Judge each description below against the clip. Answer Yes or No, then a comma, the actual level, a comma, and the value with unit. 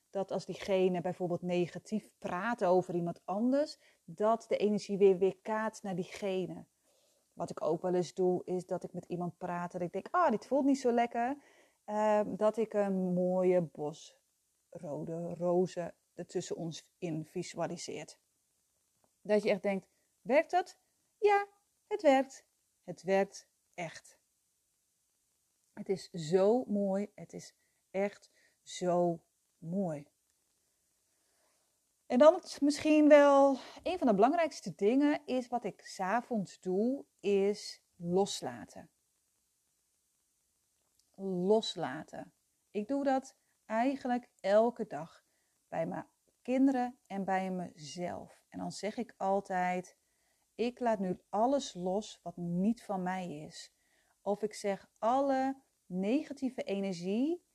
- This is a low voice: No, high, 195 Hz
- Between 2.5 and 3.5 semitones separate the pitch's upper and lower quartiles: No, average, 5.1 semitones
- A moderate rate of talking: No, slow, 130 wpm